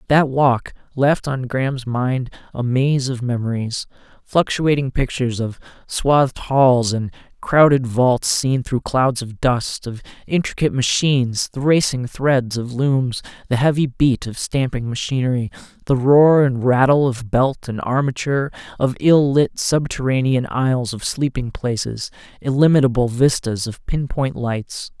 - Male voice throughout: Yes, male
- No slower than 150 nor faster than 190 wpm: No, average, 140 wpm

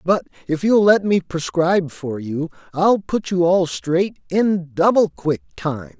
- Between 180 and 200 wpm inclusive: No, average, 170 wpm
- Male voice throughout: Yes, male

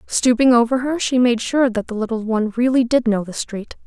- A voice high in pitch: Yes, high, 240 Hz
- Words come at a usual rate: No, fast, 235 wpm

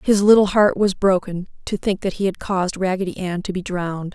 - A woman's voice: Yes, female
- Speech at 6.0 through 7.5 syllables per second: No, 5.7 syllables/s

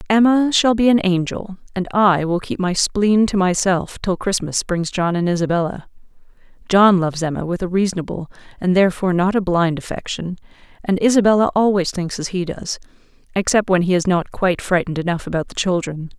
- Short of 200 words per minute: Yes, average, 180 wpm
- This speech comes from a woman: Yes, female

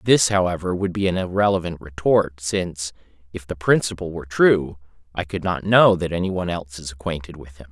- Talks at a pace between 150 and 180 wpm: No, average, 195 wpm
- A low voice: Yes, very low, 85 Hz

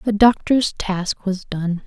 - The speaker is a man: No, female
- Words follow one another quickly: No, average, 160 wpm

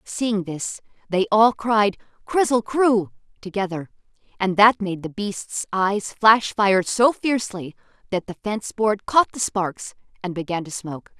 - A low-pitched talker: No, high, 205 Hz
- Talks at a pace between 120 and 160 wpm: Yes, average, 155 wpm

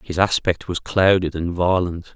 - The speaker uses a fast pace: No, average, 165 wpm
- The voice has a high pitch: No, very low, 90 Hz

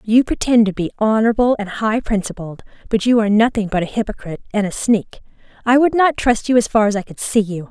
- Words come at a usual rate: No, fast, 235 wpm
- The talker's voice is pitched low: No, high, 220 Hz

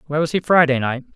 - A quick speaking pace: Yes, fast, 260 wpm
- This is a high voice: No, medium, 145 Hz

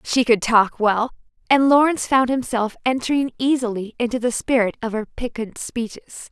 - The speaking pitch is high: Yes, high, 240 Hz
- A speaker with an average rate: Yes, average, 160 wpm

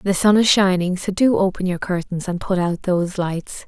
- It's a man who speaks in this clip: No, female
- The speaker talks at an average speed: No, fast, 230 wpm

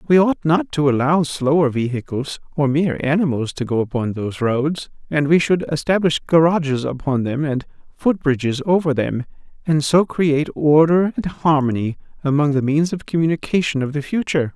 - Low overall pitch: No, medium, 150 Hz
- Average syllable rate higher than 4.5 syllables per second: Yes, 5.3 syllables/s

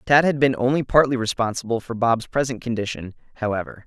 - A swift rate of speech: No, average, 170 wpm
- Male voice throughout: Yes, male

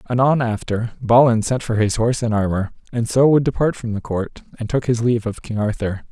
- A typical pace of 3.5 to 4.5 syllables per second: No, 5.7 syllables/s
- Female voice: No, male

